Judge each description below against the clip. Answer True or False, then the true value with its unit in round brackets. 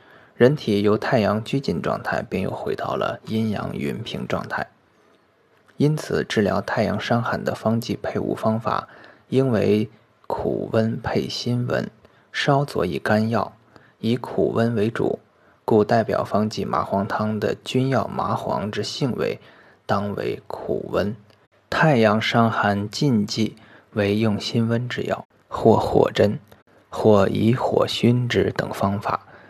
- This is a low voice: True (110 Hz)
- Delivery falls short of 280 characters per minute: True (195 characters per minute)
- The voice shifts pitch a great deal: False (2.9 semitones)